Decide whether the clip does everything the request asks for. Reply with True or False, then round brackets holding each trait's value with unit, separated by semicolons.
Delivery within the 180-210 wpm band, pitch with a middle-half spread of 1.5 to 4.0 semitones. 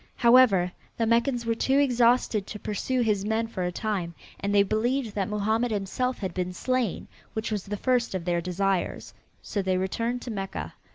True (185 wpm; 3.7 semitones)